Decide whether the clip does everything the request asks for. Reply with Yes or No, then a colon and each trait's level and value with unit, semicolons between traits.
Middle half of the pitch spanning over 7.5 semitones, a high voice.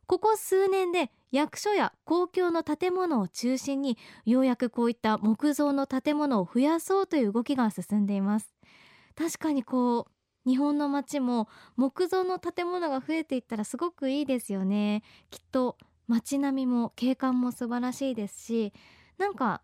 No: average, 5.2 semitones; very high, 265 Hz